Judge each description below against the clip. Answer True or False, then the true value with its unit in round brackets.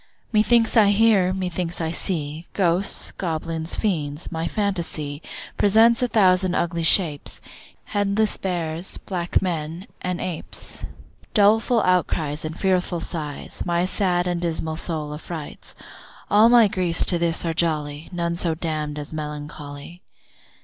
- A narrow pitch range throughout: False (3.3 semitones)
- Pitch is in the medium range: True (175 Hz)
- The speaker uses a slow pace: True (130 wpm)